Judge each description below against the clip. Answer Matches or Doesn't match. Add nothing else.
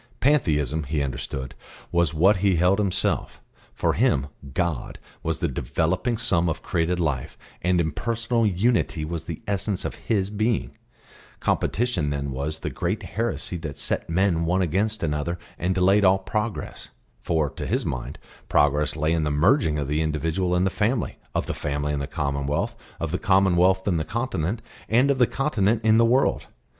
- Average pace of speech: Matches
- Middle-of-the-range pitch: Doesn't match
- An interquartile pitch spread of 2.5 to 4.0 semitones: Doesn't match